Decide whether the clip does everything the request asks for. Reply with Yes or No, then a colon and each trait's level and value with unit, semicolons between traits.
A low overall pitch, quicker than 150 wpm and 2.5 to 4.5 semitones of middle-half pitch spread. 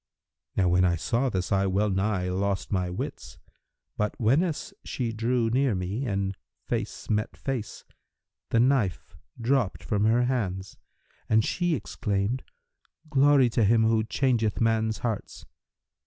No: low, 110 Hz; average, 140 wpm; average, 4.1 semitones